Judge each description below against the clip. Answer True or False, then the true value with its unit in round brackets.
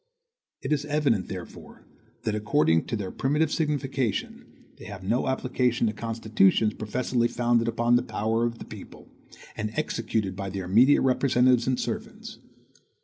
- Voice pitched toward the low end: True (115 Hz)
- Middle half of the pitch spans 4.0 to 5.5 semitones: False (3.3 semitones)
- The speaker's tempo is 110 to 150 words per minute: True (145 wpm)